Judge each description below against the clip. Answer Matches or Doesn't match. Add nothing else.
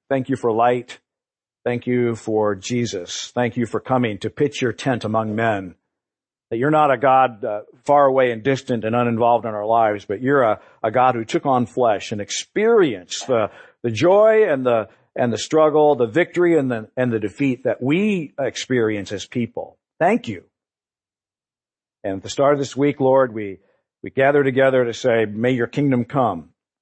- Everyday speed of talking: Matches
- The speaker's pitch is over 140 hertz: Doesn't match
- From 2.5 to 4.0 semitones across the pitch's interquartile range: Matches